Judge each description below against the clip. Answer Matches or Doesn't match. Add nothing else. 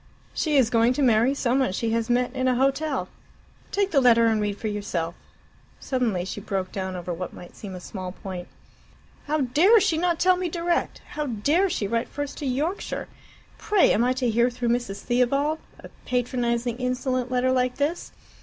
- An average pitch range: Matches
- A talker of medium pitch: Doesn't match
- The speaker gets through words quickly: Doesn't match